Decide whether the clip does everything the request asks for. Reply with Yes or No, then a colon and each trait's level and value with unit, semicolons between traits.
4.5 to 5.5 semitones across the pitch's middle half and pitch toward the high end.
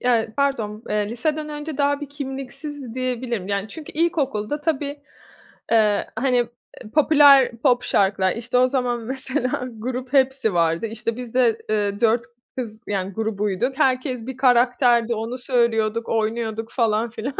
No: average, 3.3 semitones; high, 240 Hz